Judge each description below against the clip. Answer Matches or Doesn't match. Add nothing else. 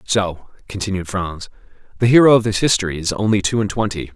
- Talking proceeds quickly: Doesn't match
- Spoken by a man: Matches